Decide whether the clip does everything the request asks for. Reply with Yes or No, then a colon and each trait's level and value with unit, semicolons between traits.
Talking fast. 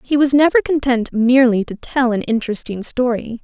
No: average, 175 wpm